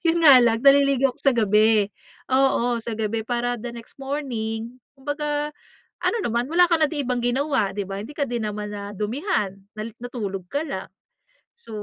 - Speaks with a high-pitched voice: Yes, high, 245 Hz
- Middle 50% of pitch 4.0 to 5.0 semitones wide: Yes, average, 4.3 semitones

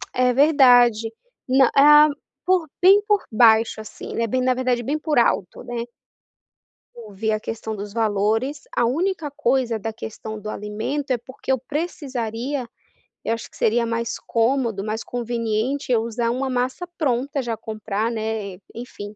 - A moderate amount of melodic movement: Yes, average, 3.4 semitones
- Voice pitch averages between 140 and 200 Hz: No, high, 240 Hz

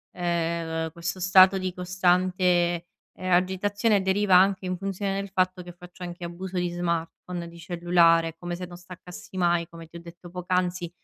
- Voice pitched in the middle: Yes, medium, 180 Hz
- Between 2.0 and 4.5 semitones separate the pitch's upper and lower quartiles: No, narrow, 1.3 semitones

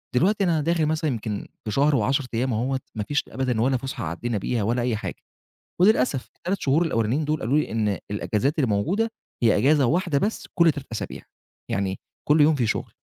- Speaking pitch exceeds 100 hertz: Yes, low, 135 Hz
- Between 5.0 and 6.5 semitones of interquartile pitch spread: Yes, wide, 5.5 semitones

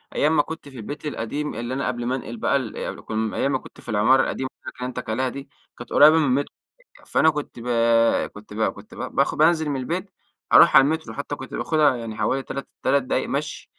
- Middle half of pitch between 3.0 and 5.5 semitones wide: Yes, average, 3.6 semitones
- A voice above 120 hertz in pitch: Yes, low, 135 Hz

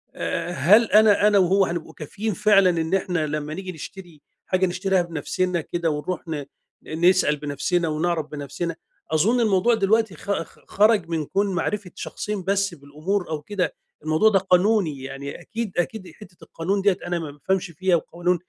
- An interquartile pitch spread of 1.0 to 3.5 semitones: No, average, 3.9 semitones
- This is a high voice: No, medium, 180 Hz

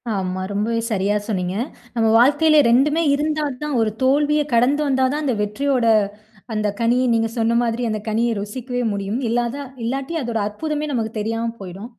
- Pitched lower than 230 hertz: No, high, 235 Hz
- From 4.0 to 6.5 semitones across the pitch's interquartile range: Yes, average, 4.3 semitones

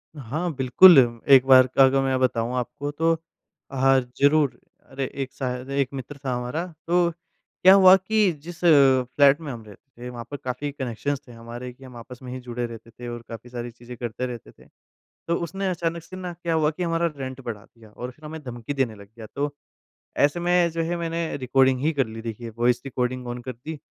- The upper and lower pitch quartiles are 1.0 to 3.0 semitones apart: No, average, 4.5 semitones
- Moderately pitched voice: No, low, 130 Hz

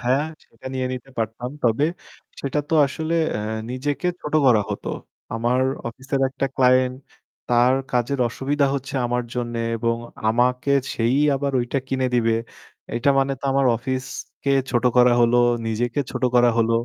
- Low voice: Yes, low, 125 Hz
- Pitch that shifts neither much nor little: No, narrow, 2.2 semitones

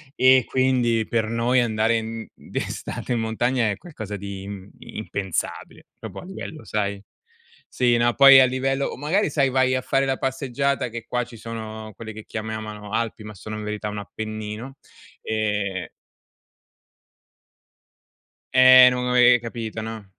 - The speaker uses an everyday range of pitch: Yes, average, 3.1 semitones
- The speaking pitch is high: No, low, 115 Hz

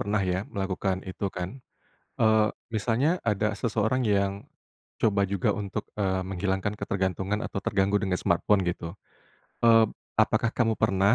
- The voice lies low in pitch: Yes, low, 100 Hz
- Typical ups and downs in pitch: No, narrow, 2.3 semitones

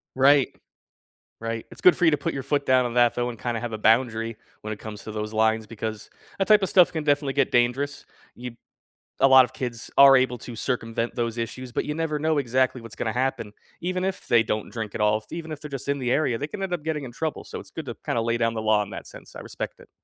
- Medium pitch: No, low, 125 Hz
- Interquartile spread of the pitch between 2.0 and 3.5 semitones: No, average, 4.0 semitones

